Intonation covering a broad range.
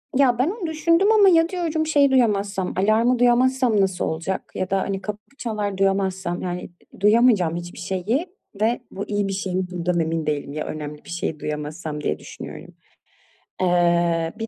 Yes: wide, 6.0 semitones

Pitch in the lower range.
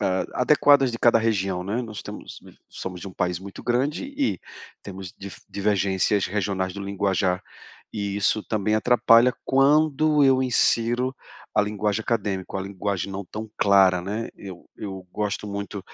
Yes: low, 105 Hz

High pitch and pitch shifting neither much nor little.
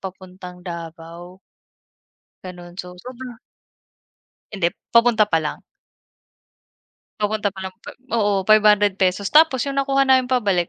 Yes: high, 195 Hz; average, 4.5 semitones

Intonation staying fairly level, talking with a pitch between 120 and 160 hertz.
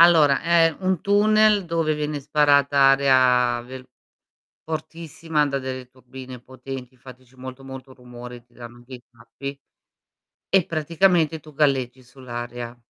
No: average, 3.8 semitones; low, 135 Hz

